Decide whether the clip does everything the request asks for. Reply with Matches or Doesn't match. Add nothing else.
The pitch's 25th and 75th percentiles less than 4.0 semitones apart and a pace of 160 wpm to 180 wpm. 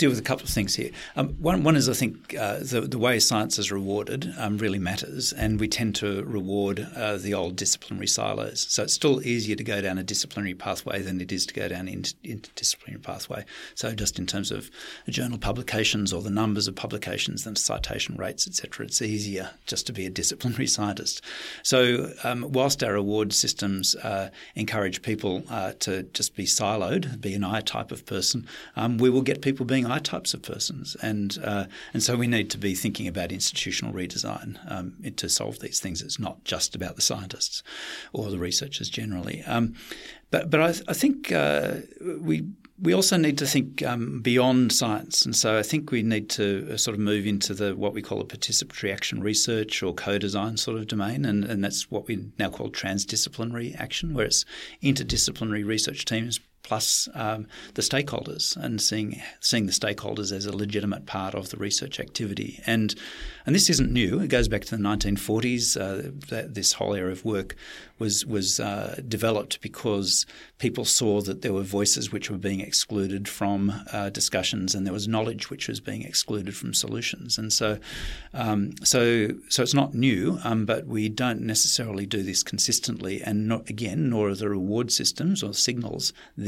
Doesn't match